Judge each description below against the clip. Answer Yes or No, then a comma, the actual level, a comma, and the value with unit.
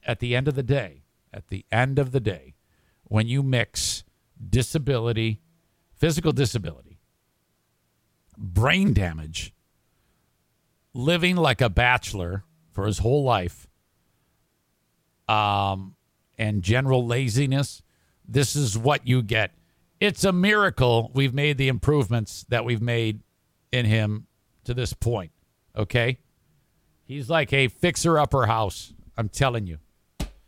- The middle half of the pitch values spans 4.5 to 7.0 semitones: Yes, average, 5.2 semitones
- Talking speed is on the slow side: Yes, slow, 125 wpm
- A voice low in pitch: Yes, low, 120 Hz